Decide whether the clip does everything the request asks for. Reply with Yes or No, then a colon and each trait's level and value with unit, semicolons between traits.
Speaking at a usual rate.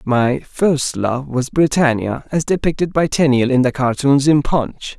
Yes: average, 170 wpm